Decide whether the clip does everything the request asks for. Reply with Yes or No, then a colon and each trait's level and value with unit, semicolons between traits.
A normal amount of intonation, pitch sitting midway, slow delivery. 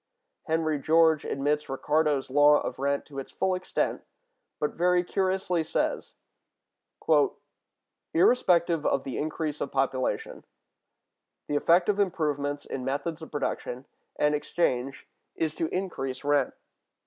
Yes: average, 3.1 semitones; medium, 150 Hz; slow, 125 wpm